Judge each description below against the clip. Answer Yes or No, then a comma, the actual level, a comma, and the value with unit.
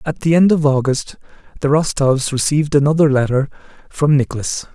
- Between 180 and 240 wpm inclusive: No, average, 150 wpm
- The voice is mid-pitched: Yes, medium, 145 Hz